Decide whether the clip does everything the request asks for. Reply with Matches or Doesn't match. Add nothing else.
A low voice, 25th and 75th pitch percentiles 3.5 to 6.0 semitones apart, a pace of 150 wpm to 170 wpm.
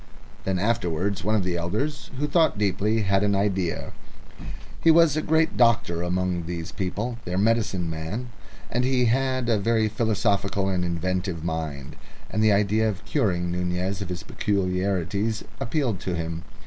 Matches